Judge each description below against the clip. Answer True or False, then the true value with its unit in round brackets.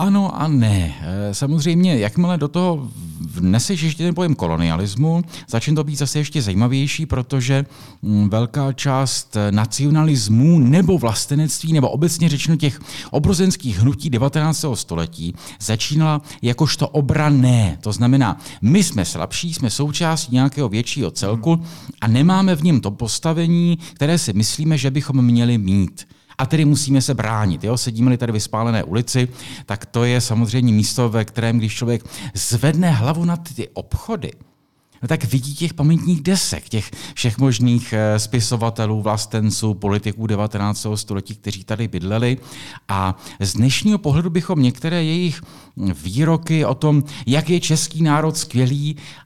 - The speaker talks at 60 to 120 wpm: False (140 wpm)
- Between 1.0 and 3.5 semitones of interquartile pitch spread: False (5.9 semitones)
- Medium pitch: False (130 Hz)